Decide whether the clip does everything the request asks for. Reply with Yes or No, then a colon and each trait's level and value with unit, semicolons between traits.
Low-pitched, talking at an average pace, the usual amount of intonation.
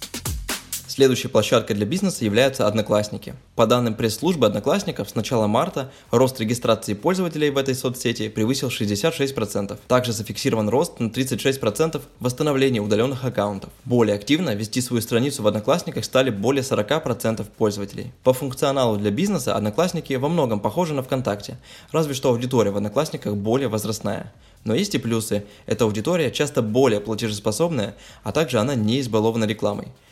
Yes: low, 120 Hz; average, 145 wpm; average, 4.1 semitones